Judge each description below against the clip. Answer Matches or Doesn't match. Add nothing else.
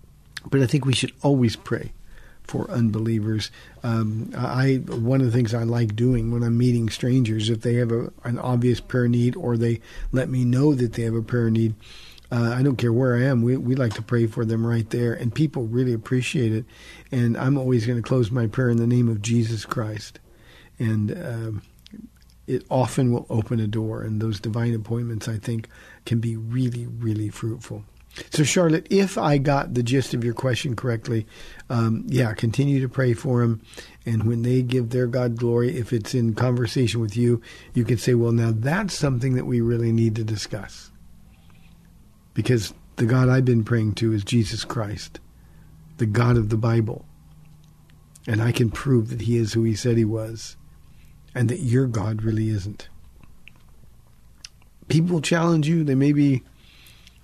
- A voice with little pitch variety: Matches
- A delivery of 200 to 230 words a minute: Doesn't match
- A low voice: Matches